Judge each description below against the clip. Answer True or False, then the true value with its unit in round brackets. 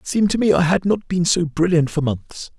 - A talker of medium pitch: True (170 Hz)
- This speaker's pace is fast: True (280 wpm)